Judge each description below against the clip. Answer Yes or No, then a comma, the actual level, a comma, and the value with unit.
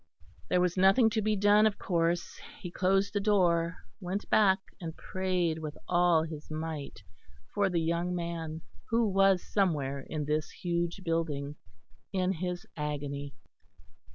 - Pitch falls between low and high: Yes, medium, 175 Hz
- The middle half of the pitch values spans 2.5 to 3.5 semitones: Yes, average, 3.2 semitones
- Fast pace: No, average, 145 wpm